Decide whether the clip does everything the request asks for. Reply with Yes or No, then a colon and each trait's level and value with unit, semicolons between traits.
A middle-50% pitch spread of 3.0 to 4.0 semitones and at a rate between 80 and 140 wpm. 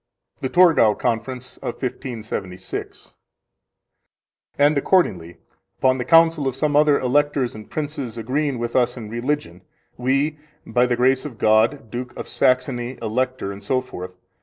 Yes: average, 3.7 semitones; slow, 135 wpm